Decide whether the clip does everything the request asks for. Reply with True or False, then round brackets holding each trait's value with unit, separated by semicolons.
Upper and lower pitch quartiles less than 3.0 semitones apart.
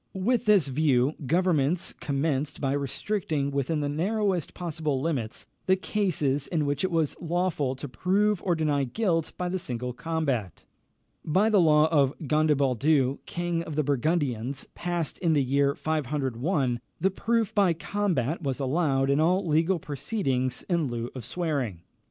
False (4.3 semitones)